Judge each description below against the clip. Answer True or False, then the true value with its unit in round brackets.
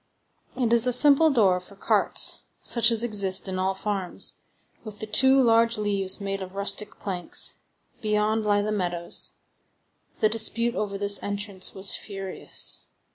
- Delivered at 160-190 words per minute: False (150 wpm)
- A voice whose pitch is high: True (205 Hz)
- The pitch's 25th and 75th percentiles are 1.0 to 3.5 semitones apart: True (2.8 semitones)